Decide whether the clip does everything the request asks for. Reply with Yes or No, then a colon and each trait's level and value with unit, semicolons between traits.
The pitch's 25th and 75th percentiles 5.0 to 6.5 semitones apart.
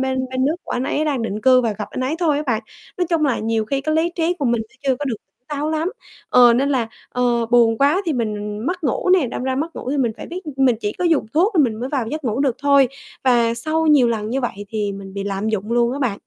No: average, 4.6 semitones